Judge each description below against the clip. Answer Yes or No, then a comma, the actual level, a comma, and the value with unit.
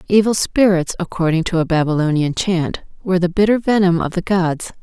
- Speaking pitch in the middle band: Yes, medium, 180 Hz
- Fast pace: No, average, 175 wpm